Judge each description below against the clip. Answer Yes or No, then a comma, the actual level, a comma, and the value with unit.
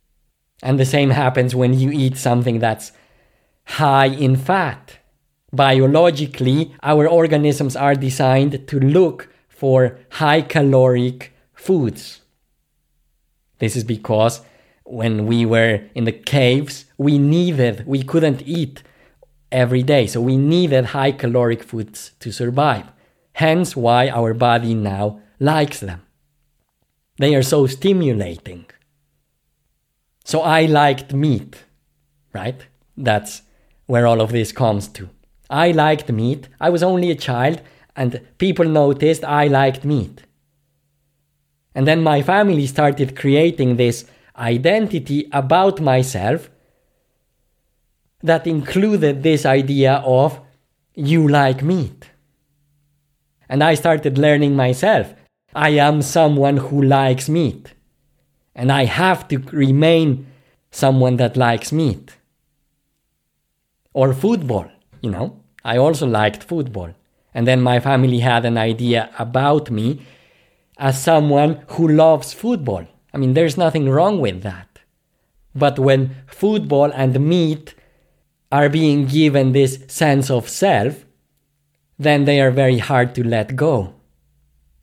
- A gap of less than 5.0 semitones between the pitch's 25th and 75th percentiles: Yes, average, 3.5 semitones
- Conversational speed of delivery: No, slow, 120 wpm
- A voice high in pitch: No, low, 135 Hz